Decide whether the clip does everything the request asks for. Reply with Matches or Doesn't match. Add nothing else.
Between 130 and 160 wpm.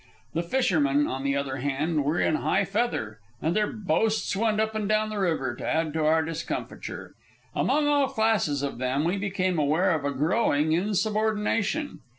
Doesn't match